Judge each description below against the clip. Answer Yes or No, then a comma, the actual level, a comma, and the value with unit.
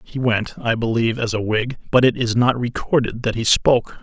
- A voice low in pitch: Yes, low, 120 Hz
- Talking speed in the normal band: No, fast, 225 wpm